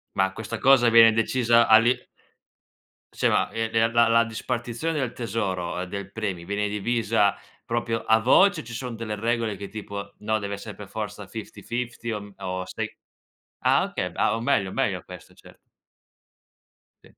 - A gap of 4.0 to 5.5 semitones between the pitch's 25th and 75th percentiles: No, narrow, 2.6 semitones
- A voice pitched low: Yes, low, 115 Hz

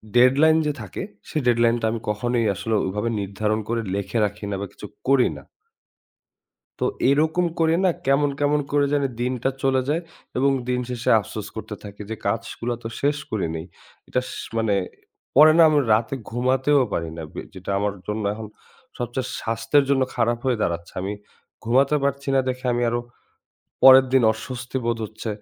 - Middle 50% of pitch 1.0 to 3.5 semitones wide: No, average, 3.9 semitones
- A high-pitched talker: No, low, 120 Hz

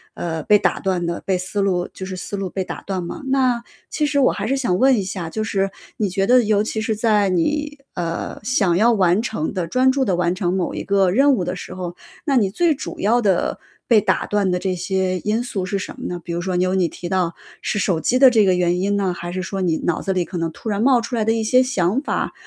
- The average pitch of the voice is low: No, high, 195 Hz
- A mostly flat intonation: No, average, 4.0 semitones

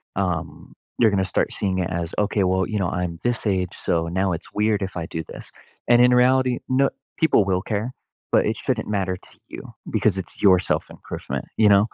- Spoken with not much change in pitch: No, average, 3.3 semitones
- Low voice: Yes, low, 100 Hz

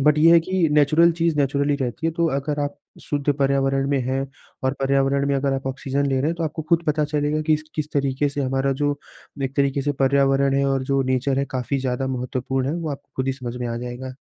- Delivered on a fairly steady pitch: Yes, narrow, 1.7 semitones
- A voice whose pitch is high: No, medium, 140 Hz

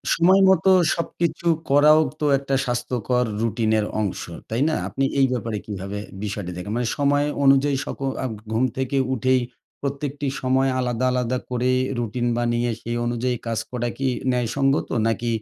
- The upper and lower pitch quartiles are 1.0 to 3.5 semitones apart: Yes, average, 2.9 semitones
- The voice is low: Yes, low, 125 Hz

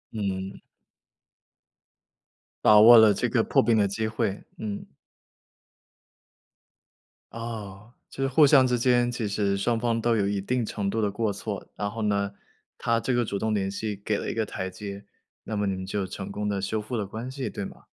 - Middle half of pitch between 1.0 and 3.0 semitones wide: Yes, narrow, 2.5 semitones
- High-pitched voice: No, low, 105 Hz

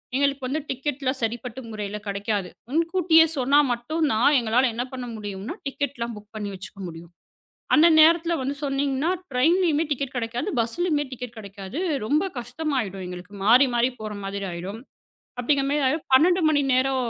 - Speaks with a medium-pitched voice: No, very high, 255 Hz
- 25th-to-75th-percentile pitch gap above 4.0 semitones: Yes, average, 5.2 semitones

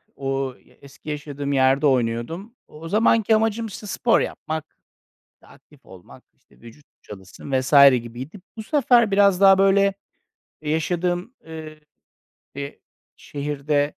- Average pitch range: No, wide, 6.3 semitones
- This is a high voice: No, medium, 155 Hz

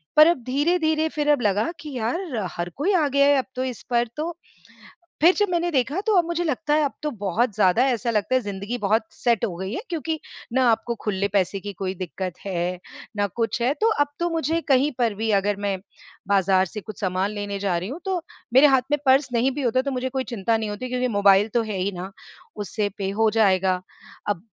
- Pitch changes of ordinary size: No, wide, 6.2 semitones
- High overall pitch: Yes, high, 235 Hz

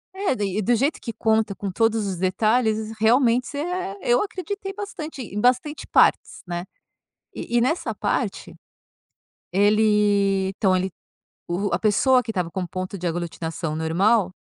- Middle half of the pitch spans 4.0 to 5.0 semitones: Yes, average, 4.7 semitones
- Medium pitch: No, high, 215 Hz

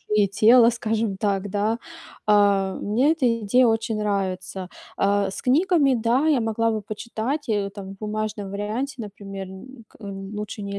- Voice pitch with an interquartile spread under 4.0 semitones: Yes, average, 2.7 semitones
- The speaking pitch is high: Yes, high, 215 Hz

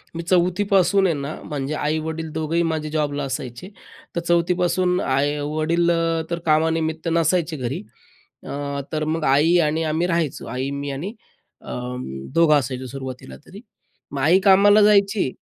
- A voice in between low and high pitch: Yes, medium, 160 Hz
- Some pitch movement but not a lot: Yes, average, 3.1 semitones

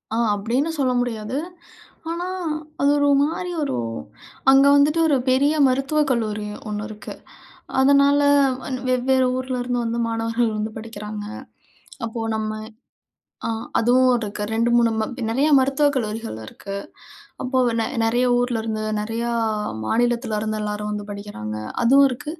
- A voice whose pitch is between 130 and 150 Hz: No, high, 240 Hz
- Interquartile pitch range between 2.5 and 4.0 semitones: Yes, average, 3.6 semitones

